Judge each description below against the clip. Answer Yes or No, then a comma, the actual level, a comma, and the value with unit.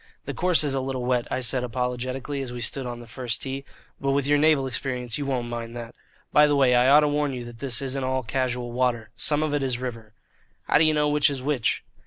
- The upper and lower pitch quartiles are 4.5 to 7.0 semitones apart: No, narrow, 2.6 semitones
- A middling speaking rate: No, fast, 255 wpm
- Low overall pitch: Yes, low, 130 Hz